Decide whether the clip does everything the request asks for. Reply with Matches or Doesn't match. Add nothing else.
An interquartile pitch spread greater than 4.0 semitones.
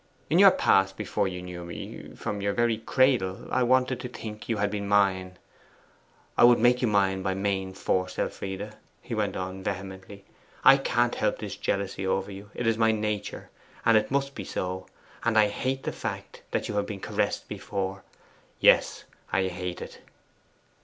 Doesn't match